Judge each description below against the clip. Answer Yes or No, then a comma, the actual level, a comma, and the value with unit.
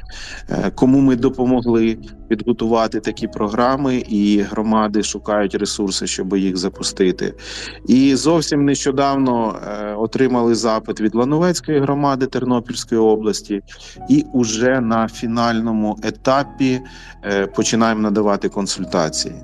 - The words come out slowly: Yes, slow, 95 wpm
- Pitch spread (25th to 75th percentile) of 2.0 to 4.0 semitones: Yes, average, 3.7 semitones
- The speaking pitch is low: Yes, low, 115 Hz